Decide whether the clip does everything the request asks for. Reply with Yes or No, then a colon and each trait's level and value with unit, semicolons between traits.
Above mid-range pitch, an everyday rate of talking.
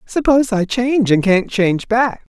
Yes: high, 220 Hz; average, 180 wpm